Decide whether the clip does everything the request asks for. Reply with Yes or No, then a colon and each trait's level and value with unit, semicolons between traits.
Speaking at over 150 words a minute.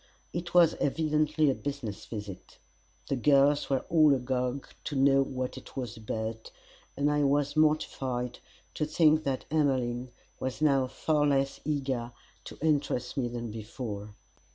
No: average, 145 wpm